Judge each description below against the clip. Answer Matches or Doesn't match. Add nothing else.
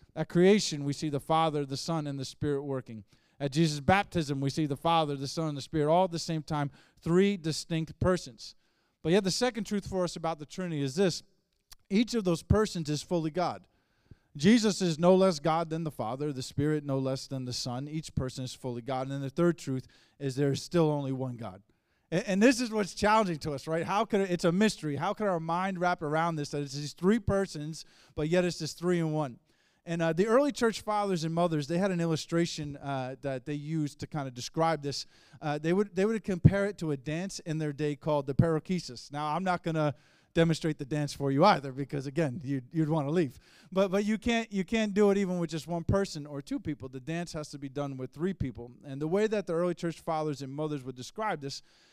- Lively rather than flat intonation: Doesn't match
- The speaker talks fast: Matches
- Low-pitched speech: Doesn't match